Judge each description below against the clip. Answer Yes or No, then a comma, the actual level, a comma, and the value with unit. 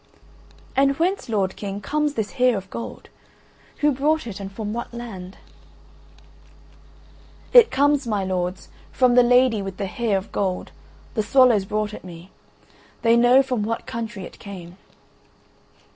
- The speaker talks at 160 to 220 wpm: No, average, 150 wpm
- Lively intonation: No, average, 4.7 semitones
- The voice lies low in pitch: No, high, 225 Hz